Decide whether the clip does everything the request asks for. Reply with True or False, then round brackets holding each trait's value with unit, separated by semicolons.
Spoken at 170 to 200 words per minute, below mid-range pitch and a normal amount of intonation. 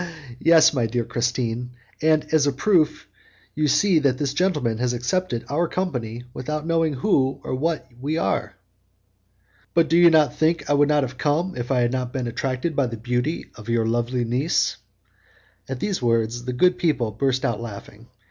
True (175 wpm; 130 Hz; 4.7 semitones)